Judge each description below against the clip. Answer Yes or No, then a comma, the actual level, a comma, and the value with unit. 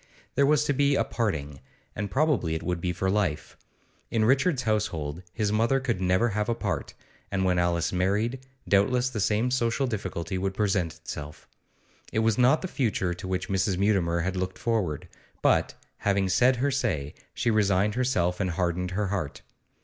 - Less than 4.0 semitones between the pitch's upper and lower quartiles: No, average, 4.7 semitones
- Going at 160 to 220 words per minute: Yes, average, 180 wpm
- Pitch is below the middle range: Yes, low, 100 Hz